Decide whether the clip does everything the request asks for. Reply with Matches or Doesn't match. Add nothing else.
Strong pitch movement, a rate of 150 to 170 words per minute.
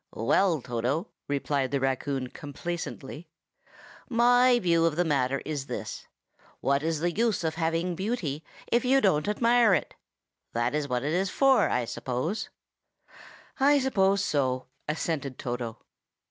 Doesn't match